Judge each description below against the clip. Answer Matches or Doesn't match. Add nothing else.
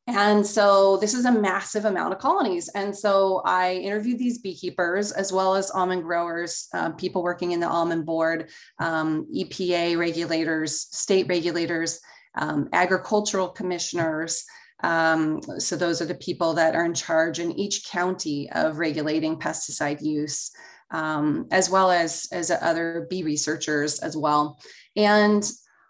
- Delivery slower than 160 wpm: Matches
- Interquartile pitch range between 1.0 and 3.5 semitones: Matches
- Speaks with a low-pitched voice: Doesn't match